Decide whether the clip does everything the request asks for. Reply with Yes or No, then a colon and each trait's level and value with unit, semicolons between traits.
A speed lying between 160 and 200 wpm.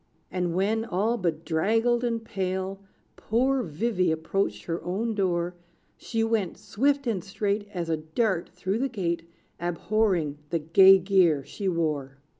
No: average, 140 wpm